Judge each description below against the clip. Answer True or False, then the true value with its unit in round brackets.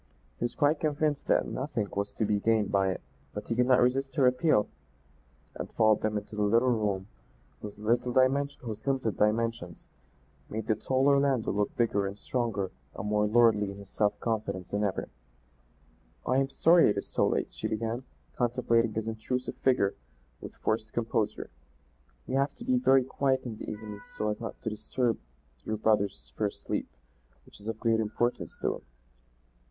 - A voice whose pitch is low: True (110 Hz)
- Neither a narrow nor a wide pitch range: True (3.4 semitones)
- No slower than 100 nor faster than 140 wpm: False (175 wpm)